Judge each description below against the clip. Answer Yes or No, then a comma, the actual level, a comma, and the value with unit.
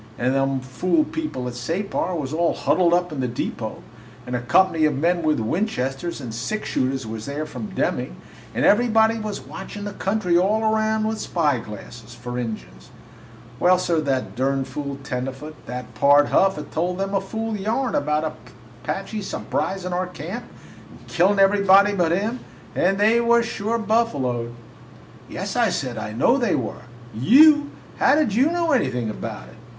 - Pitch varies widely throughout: Yes, wide, 8.4 semitones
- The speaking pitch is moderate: Yes, medium, 170 Hz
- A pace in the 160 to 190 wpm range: Yes, average, 170 wpm